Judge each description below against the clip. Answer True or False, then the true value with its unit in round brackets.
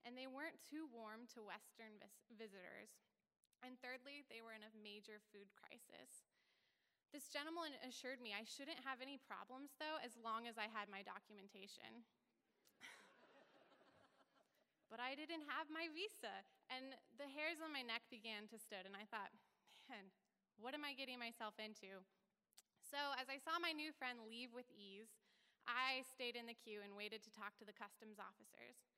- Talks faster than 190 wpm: False (170 wpm)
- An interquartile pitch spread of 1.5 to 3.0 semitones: False (4.3 semitones)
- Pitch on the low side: False (235 Hz)